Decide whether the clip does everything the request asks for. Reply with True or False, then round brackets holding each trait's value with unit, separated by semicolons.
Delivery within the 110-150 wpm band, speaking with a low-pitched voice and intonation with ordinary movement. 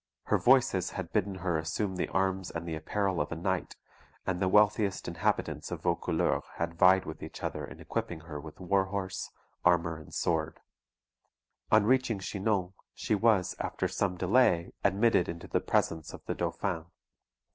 False (165 wpm; 95 Hz; 3.1 semitones)